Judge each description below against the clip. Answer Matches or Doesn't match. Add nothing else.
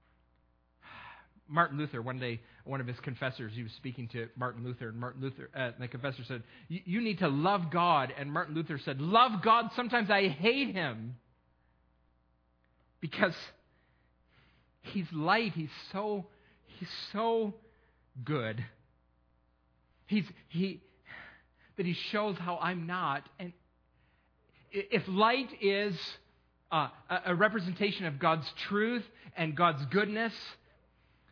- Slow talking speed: Matches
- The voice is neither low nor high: Matches